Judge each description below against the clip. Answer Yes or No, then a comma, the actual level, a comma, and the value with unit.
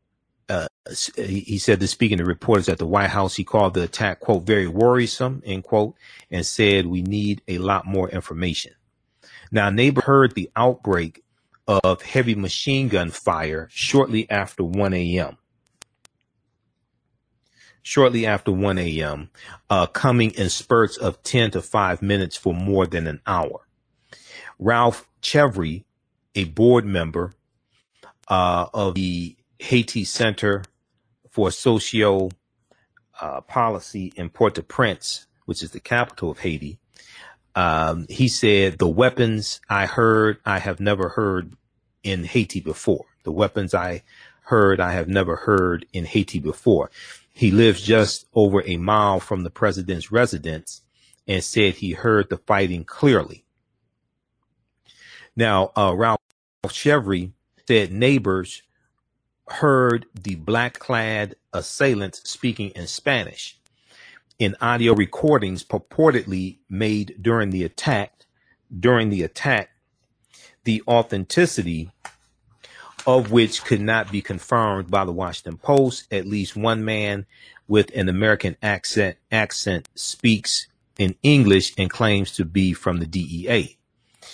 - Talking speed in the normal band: No, slow, 130 wpm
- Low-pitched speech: Yes, low, 100 Hz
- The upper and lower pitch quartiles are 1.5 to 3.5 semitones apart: No, average, 3.9 semitones